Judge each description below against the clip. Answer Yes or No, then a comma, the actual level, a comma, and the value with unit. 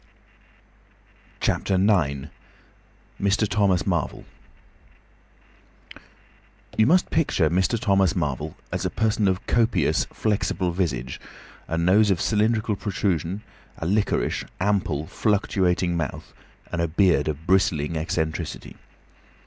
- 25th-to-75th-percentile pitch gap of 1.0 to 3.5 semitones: No, average, 4.0 semitones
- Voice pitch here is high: No, very low, 95 Hz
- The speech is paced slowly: Yes, slow, 105 wpm